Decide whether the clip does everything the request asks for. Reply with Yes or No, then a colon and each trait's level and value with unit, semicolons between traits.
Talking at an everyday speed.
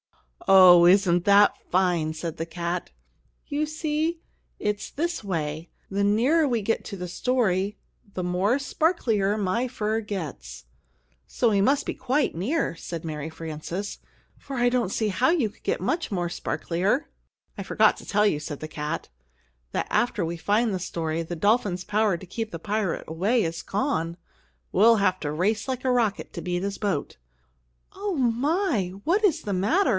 Yes: average, 170 wpm